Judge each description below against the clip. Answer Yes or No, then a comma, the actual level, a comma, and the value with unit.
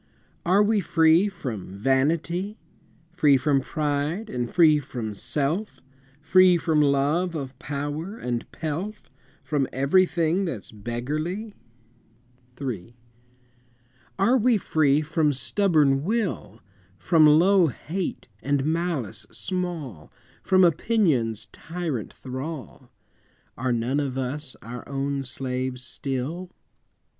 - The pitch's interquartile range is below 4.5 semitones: No, average, 5.2 semitones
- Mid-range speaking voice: Yes, medium, 150 Hz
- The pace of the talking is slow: Yes, slow, 105 wpm